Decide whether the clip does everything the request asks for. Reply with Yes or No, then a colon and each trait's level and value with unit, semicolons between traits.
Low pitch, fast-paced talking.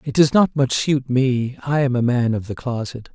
Yes: low, 130 Hz; fast, 250 wpm